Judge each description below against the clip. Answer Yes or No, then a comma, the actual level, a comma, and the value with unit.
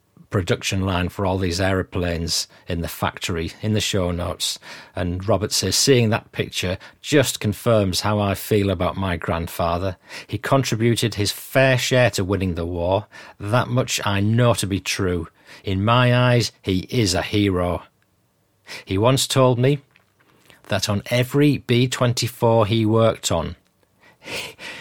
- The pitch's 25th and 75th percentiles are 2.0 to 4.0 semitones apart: No, average, 4.7 semitones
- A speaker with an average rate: Yes, average, 150 wpm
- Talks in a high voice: No, low, 105 Hz